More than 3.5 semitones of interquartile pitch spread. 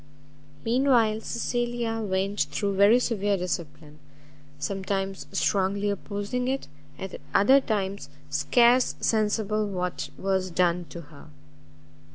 No: average, 3.2 semitones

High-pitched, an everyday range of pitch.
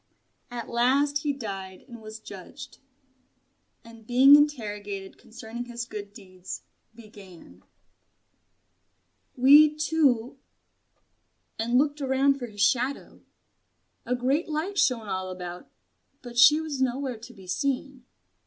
Yes: high, 245 Hz; average, 4.9 semitones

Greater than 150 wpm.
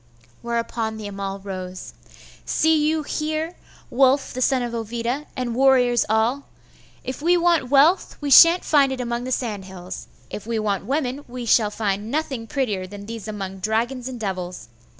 Yes: average, 170 wpm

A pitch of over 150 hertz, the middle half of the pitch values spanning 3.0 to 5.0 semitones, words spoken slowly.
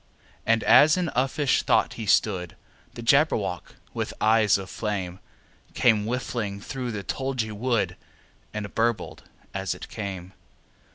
No: low, 110 Hz; average, 3.9 semitones; slow, 130 wpm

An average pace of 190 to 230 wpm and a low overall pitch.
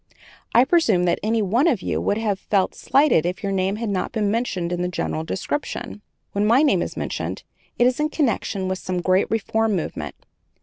No: fast, 205 wpm; high, 200 Hz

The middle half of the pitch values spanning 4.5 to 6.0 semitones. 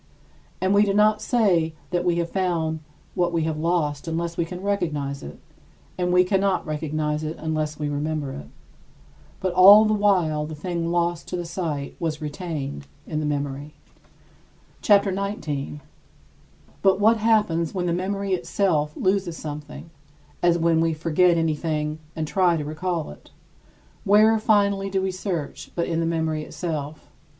No: average, 3.5 semitones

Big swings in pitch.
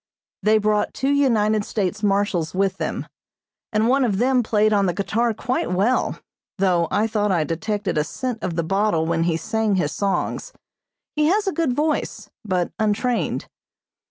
No: average, 4.1 semitones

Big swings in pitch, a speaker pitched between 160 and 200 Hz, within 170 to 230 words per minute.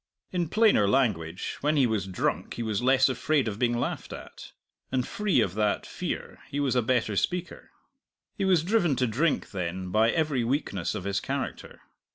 No: wide, 6.5 semitones; low, 125 Hz; average, 185 wpm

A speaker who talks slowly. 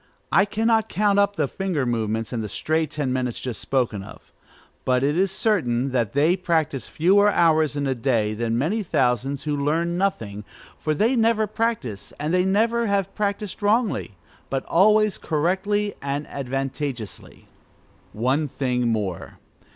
No: average, 150 wpm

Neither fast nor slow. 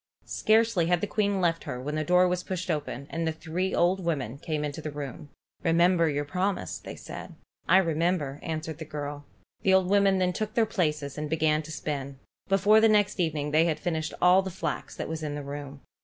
No: fast, 215 wpm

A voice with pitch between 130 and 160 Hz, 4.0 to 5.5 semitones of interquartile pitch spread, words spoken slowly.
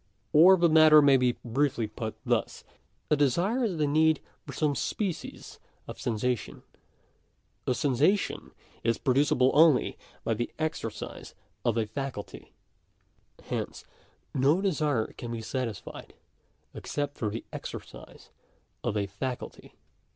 Yes: low, 135 Hz; average, 4.9 semitones; slow, 130 wpm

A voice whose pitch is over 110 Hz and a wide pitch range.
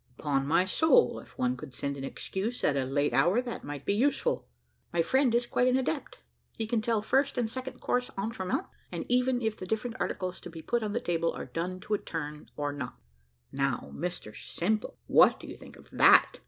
Yes: high, 190 Hz; wide, 8.6 semitones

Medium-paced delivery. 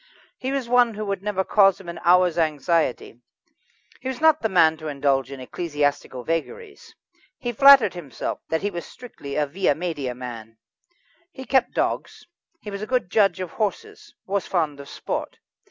Yes: average, 175 wpm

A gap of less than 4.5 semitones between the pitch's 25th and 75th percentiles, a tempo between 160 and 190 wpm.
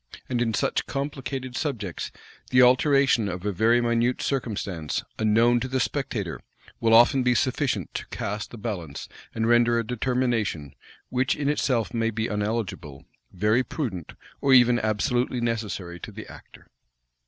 No: average, 3.3 semitones; average, 150 wpm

